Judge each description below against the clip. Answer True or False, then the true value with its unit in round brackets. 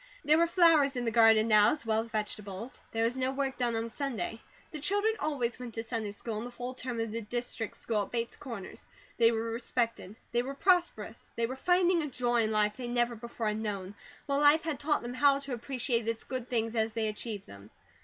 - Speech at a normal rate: False (230 wpm)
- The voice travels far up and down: False (3.3 semitones)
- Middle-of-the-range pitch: False (235 Hz)